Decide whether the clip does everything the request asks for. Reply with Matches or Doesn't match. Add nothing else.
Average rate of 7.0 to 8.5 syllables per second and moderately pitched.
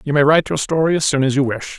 Matches